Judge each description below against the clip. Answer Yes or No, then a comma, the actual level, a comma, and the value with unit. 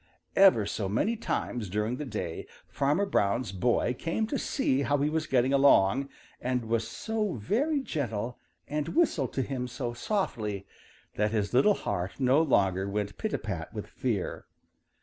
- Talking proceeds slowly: No, average, 160 wpm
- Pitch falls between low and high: No, low, 125 Hz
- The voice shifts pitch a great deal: Yes, wide, 6.3 semitones